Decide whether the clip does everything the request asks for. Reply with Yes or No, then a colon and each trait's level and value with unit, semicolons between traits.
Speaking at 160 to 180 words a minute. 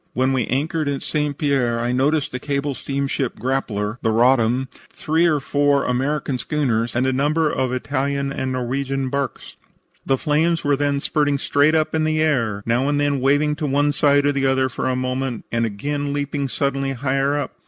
No: average, 190 wpm